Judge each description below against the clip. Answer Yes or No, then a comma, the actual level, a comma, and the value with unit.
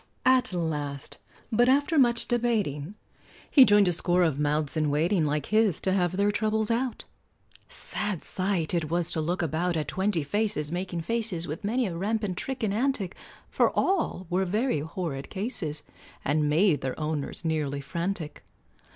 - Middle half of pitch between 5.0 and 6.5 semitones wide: Yes, wide, 5.5 semitones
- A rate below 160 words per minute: No, average, 165 wpm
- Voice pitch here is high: No, medium, 180 Hz